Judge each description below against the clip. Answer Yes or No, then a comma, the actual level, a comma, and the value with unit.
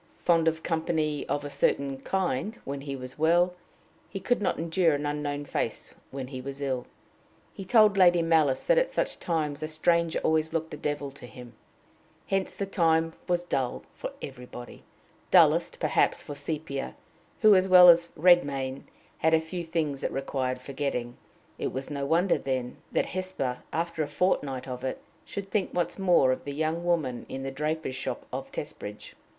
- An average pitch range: Yes, average, 4.1 semitones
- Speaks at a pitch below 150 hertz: No, medium, 155 Hz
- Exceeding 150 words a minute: Yes, average, 180 wpm